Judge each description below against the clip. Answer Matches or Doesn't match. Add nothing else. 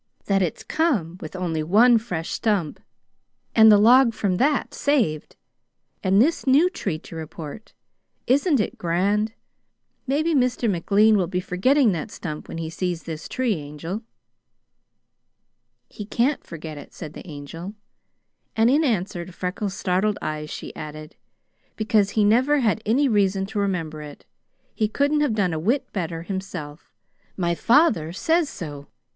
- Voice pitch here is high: Matches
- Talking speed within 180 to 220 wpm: Doesn't match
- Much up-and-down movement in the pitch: Matches